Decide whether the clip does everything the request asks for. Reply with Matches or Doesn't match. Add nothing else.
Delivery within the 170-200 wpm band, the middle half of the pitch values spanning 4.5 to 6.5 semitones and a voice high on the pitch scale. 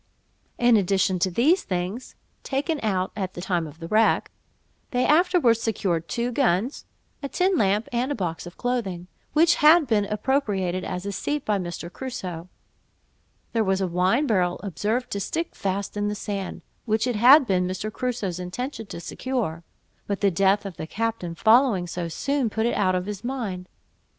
Matches